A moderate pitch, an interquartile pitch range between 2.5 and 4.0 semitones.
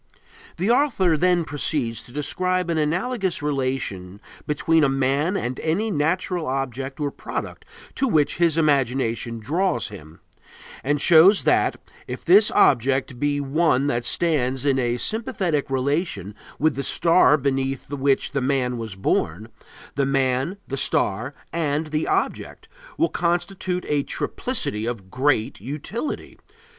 No: medium, 145 Hz; average, 4.7 semitones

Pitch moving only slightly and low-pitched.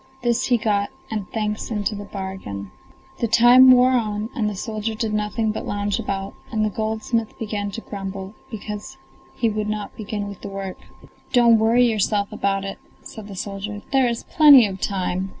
No: narrow, 2.2 semitones; high, 210 Hz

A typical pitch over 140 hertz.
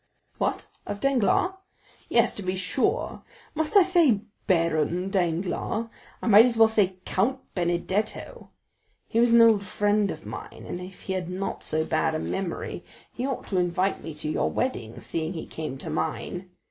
Yes: high, 190 Hz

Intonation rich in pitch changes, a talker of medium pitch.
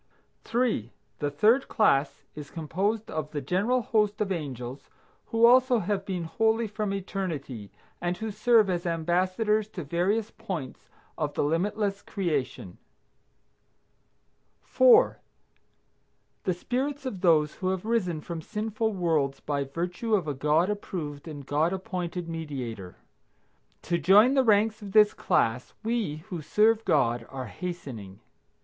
Yes: wide, 6.1 semitones; medium, 180 Hz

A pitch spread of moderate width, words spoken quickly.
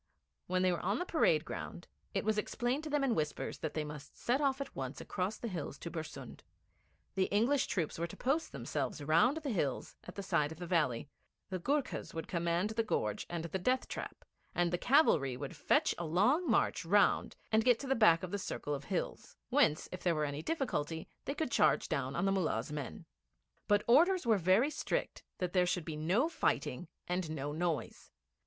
No: wide, 7.2 semitones; fast, 210 wpm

